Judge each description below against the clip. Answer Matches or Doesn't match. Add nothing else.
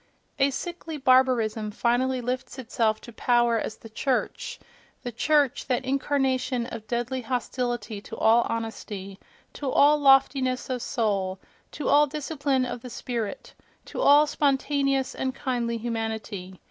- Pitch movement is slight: Doesn't match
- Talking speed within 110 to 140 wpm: Matches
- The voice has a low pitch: Doesn't match